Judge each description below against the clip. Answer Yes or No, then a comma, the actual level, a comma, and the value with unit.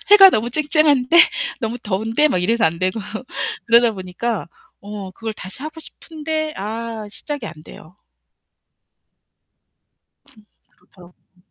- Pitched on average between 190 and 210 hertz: No, high, 225 Hz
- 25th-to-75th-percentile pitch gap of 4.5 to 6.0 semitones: No, wide, 6.7 semitones